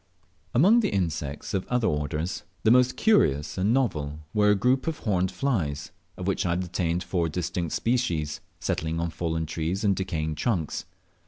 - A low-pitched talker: Yes, very low, 90 Hz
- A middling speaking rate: Yes, average, 165 wpm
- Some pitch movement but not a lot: No, wide, 5.7 semitones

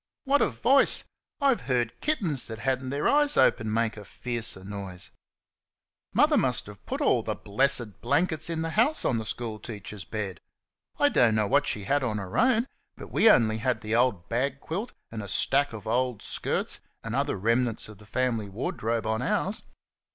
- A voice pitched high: No, low, 120 Hz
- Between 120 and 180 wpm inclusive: No, average, 190 wpm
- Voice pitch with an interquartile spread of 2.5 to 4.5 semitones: No, average, 4.9 semitones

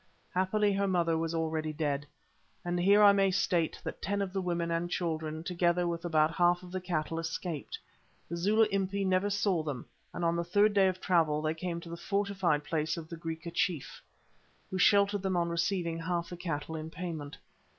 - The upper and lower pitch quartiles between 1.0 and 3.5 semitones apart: Yes, narrow, 2.5 semitones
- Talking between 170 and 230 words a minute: Yes, average, 200 wpm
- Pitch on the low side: No, medium, 175 Hz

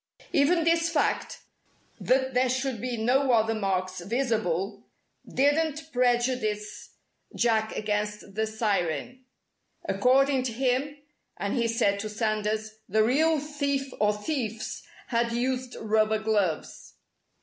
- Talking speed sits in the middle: No, slow, 115 wpm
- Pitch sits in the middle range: No, high, 235 Hz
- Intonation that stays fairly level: No, average, 3.7 semitones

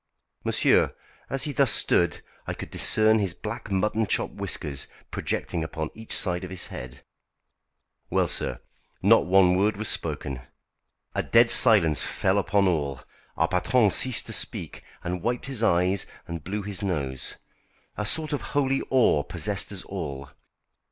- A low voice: Yes, very low, 95 Hz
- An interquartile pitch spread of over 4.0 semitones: Yes, average, 4.6 semitones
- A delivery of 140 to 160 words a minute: Yes, average, 155 wpm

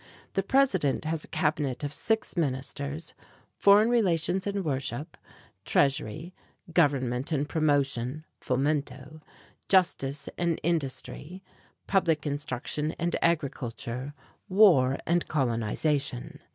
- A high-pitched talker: No, medium, 150 Hz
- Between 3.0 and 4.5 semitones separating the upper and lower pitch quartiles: Yes, average, 4.1 semitones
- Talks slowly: Yes, slow, 100 wpm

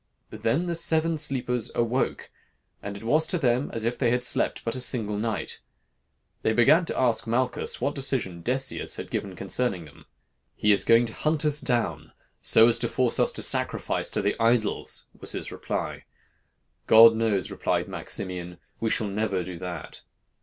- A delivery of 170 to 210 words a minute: Yes, average, 175 wpm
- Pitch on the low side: Yes, low, 115 Hz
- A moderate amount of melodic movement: Yes, average, 3.7 semitones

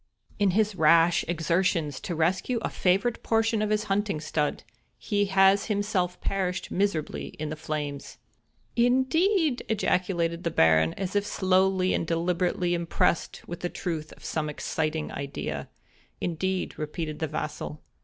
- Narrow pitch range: No, average, 4.3 semitones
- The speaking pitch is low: No, medium, 180 Hz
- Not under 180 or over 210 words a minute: No, average, 160 wpm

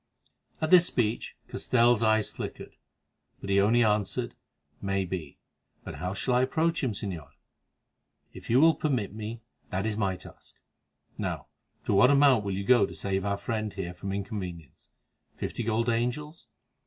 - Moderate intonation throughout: Yes, average, 3.9 semitones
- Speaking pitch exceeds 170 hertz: No, low, 110 Hz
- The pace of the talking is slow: No, average, 160 wpm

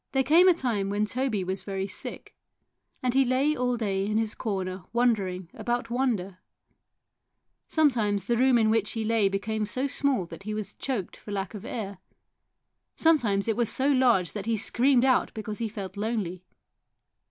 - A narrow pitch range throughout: No, average, 4.1 semitones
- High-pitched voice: Yes, high, 220 Hz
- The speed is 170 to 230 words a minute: Yes, average, 180 wpm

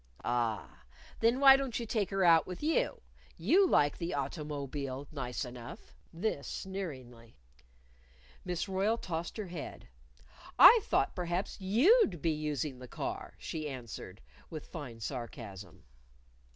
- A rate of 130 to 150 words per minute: Yes, average, 140 wpm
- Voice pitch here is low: No, medium, 160 Hz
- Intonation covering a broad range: Yes, wide, 7.3 semitones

